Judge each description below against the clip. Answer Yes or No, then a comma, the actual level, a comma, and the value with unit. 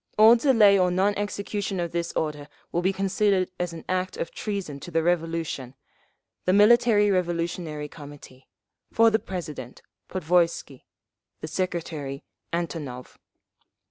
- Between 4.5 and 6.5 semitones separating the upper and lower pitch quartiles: No, average, 4.0 semitones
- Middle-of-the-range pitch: Yes, medium, 175 Hz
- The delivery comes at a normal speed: No, slow, 130 wpm